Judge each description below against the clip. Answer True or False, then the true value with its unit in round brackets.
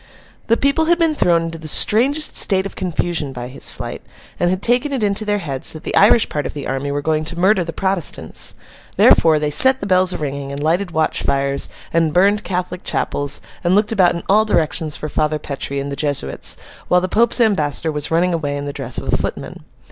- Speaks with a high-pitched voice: False (170 Hz)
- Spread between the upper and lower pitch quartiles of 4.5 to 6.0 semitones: True (5.4 semitones)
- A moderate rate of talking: False (225 wpm)